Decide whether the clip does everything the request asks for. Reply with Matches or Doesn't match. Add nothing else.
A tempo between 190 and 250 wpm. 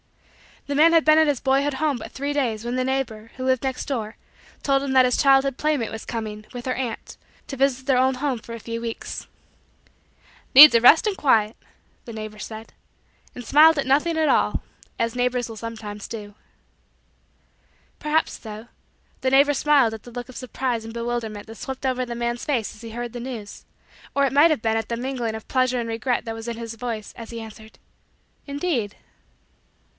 Matches